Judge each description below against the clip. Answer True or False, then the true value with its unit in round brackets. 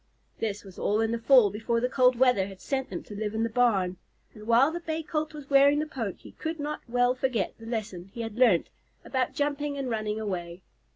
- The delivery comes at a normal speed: False (230 wpm)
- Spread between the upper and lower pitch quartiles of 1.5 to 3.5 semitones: False (4.6 semitones)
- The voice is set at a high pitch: True (235 Hz)